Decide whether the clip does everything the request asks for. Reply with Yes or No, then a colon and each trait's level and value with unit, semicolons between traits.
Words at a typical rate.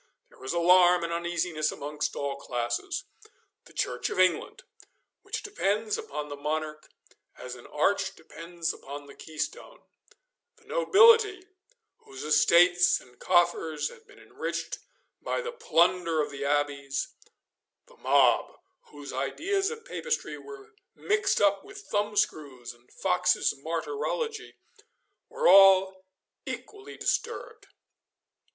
No: slow, 120 wpm